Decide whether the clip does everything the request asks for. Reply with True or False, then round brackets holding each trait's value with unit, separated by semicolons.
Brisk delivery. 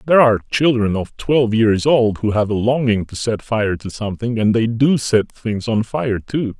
True (220 wpm)